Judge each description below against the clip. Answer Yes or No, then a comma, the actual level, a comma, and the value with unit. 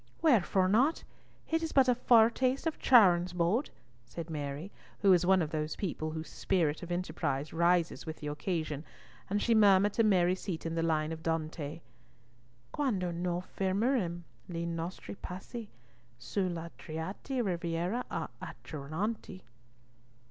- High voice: No, medium, 175 Hz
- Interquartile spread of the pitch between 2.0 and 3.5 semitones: No, average, 4.2 semitones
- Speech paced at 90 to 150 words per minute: Yes, average, 140 wpm